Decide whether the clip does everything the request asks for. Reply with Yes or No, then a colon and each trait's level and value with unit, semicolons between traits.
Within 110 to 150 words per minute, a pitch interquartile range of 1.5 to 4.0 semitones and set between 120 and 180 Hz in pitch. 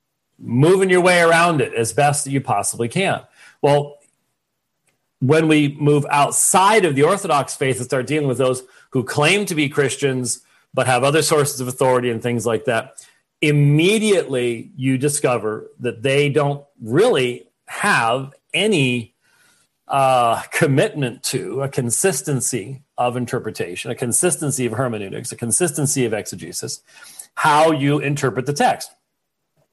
Yes: average, 140 wpm; average, 3.0 semitones; medium, 140 Hz